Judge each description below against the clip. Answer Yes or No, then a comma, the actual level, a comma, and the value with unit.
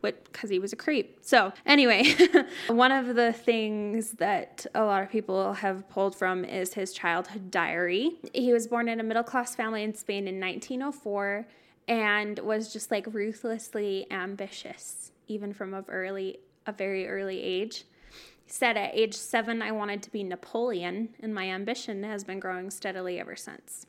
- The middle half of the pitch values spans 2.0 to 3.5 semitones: Yes, average, 3.0 semitones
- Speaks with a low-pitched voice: No, high, 210 Hz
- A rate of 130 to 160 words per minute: No, average, 170 wpm